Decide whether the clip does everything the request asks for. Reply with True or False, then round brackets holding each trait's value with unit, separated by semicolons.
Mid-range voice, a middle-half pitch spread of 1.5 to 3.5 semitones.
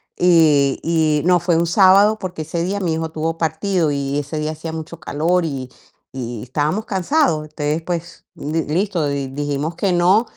True (160 Hz; 3.2 semitones)